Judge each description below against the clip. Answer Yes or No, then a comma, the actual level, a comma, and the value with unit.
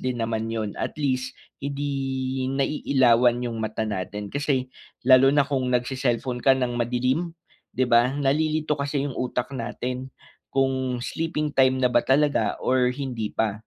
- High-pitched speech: No, low, 130 Hz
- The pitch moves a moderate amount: No, narrow, 2.2 semitones